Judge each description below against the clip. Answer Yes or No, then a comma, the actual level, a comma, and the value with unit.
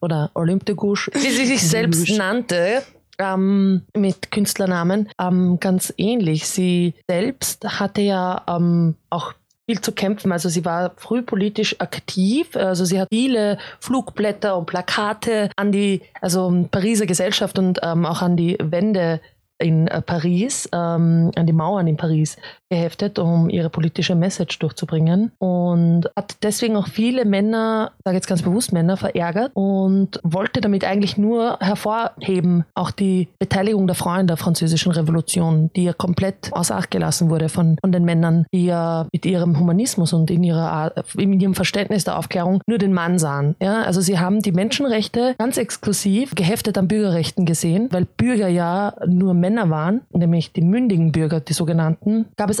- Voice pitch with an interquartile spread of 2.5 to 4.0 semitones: Yes, average, 3.1 semitones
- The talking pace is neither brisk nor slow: Yes, average, 160 wpm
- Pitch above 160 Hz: Yes, medium, 185 Hz